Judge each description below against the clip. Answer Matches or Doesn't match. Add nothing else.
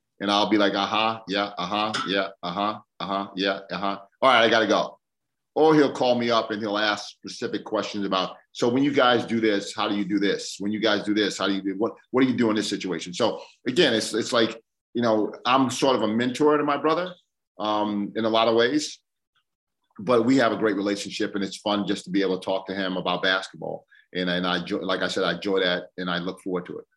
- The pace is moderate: Doesn't match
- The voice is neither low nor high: Doesn't match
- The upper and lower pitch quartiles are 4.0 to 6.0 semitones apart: Doesn't match